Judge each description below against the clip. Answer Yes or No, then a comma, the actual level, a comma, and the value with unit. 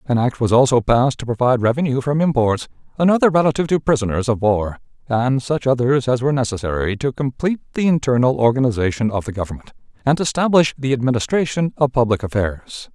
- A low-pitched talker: Yes, low, 125 Hz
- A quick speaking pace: No, average, 170 wpm